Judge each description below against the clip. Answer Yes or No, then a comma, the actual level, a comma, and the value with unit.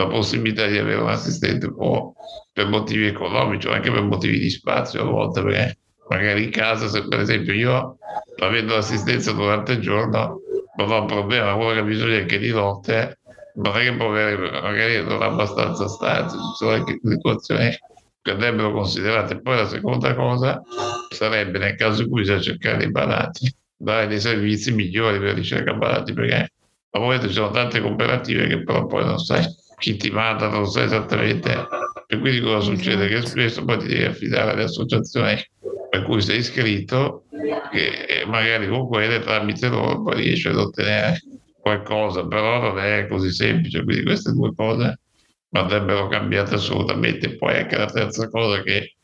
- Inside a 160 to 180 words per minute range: Yes, fast, 170 wpm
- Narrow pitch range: Yes, narrow, 2.2 semitones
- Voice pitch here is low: Yes, low, 110 Hz